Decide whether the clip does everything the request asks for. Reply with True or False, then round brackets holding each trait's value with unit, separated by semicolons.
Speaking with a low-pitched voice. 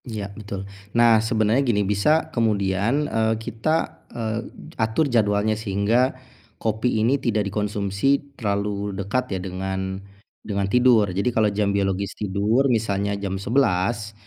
True (105 Hz)